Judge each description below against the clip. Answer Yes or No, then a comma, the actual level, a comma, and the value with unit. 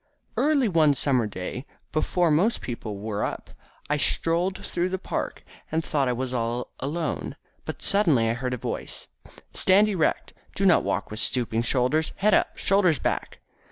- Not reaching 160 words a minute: No, average, 165 wpm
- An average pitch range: No, wide, 6.9 semitones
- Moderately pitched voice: Yes, medium, 150 Hz